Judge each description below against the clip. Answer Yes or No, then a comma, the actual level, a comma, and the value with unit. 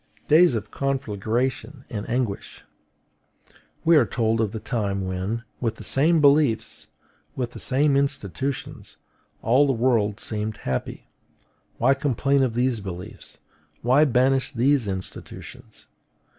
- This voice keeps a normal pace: No, slow, 125 wpm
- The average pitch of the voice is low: Yes, low, 120 Hz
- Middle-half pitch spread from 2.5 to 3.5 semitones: No, average, 4.1 semitones